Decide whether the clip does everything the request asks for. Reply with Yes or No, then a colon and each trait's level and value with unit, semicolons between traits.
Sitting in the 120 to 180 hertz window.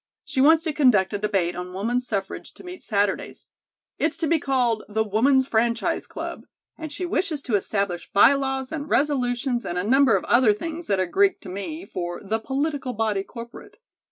No: high, 245 Hz